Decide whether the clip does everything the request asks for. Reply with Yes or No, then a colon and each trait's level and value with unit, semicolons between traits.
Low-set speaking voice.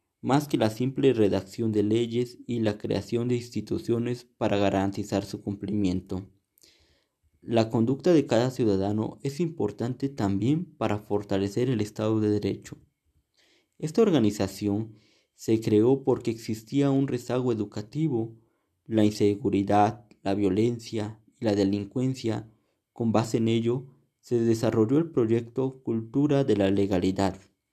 Yes: low, 110 Hz